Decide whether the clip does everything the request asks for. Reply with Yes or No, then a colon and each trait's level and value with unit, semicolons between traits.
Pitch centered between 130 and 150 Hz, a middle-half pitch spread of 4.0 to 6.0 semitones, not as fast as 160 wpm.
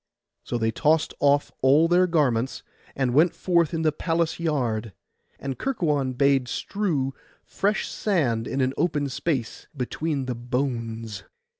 Yes: medium, 140 Hz; average, 4.8 semitones; average, 140 wpm